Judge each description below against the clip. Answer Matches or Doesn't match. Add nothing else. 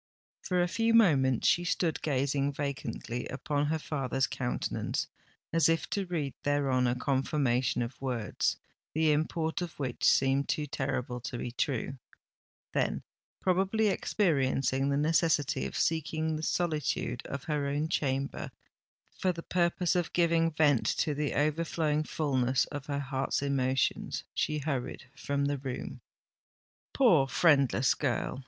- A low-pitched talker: Doesn't match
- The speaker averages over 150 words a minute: Doesn't match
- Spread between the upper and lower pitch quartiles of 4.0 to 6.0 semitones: Doesn't match